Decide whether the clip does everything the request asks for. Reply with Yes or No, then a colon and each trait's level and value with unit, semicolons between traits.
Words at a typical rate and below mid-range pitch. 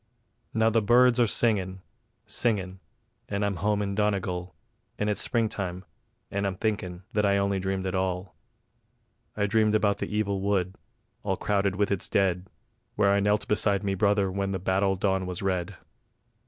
Yes: average, 170 wpm; low, 100 Hz